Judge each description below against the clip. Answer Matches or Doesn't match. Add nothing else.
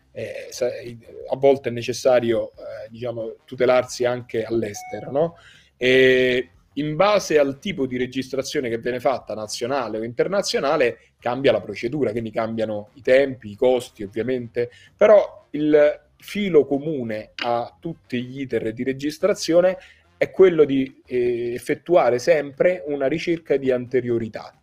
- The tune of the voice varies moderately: Doesn't match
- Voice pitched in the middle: Doesn't match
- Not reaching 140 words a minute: Matches